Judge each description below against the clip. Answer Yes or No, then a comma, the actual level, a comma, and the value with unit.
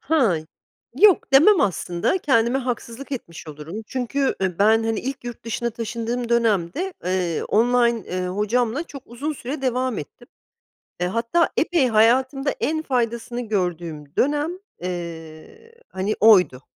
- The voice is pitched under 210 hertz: No, high, 235 Hz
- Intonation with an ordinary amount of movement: No, wide, 6.2 semitones